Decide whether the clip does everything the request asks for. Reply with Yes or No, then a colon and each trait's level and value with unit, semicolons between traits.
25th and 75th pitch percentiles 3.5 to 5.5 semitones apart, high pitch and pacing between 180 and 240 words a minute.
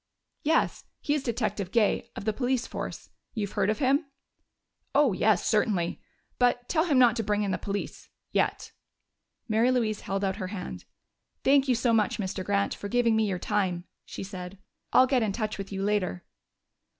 Yes: average, 3.8 semitones; high, 215 Hz; average, 185 wpm